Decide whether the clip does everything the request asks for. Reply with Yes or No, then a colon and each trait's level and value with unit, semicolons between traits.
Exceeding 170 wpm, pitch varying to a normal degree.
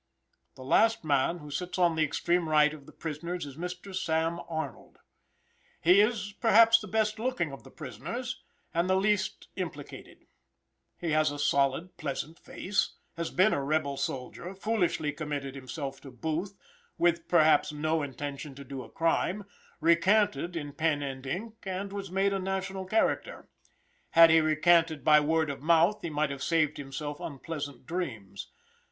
No: average, 160 wpm; average, 4.3 semitones